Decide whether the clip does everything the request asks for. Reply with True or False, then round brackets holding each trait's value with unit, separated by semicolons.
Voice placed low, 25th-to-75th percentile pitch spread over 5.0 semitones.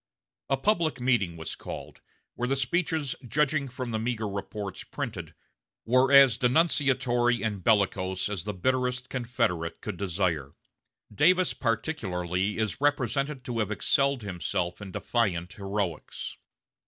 True (115 Hz; 5.4 semitones)